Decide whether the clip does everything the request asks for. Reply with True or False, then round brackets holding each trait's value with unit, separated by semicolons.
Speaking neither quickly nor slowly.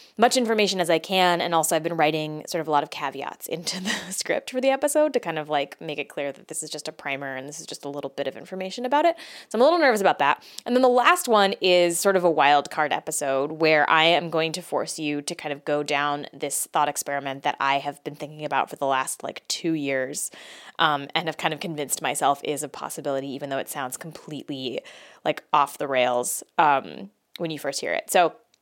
False (245 wpm)